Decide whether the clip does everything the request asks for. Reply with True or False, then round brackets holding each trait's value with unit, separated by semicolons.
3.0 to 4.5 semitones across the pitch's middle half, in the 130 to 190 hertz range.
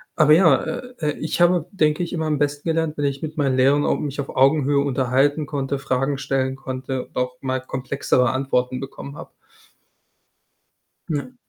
False (2.5 semitones; 140 Hz)